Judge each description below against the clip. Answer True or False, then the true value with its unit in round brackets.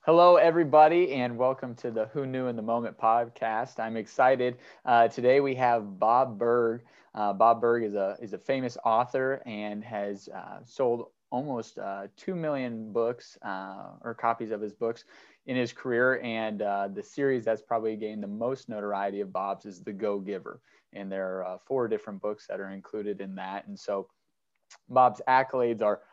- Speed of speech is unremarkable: True (185 wpm)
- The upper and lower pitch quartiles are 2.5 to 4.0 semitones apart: True (3.6 semitones)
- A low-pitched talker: True (115 Hz)